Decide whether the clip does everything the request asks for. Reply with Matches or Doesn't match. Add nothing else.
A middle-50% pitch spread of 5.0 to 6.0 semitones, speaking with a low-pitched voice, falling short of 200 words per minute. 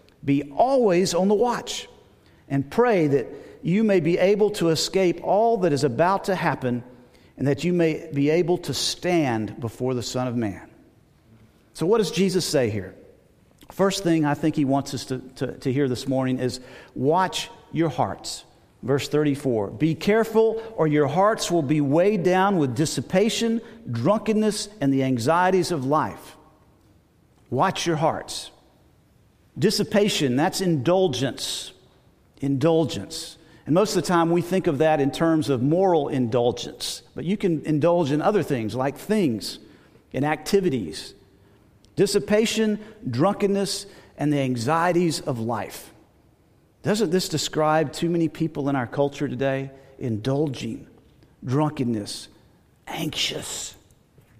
Doesn't match